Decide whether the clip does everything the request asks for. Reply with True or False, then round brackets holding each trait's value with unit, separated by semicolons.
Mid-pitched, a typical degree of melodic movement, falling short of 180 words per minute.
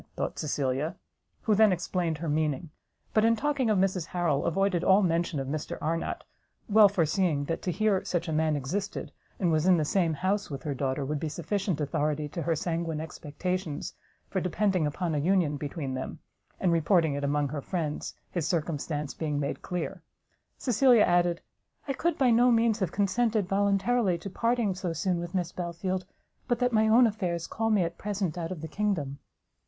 False (175 Hz; 4.6 semitones; 190 wpm)